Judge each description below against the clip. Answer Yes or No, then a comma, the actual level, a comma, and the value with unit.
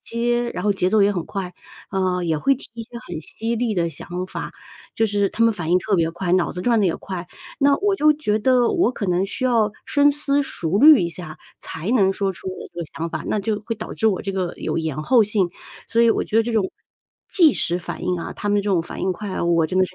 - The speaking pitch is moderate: No, high, 200 Hz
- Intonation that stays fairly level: No, average, 4.5 semitones